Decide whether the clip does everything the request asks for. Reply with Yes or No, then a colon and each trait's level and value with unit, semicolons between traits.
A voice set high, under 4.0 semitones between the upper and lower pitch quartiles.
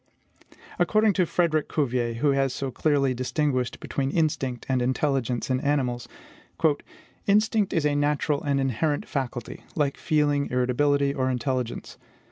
No: medium, 140 Hz; average, 2.7 semitones